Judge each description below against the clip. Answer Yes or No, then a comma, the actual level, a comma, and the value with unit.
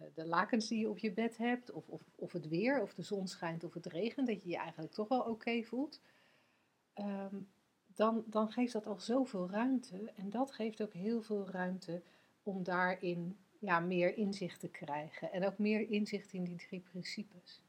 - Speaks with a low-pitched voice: No, high, 195 Hz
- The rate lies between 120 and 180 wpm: No, fast, 200 wpm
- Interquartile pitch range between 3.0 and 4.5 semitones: Yes, average, 3.6 semitones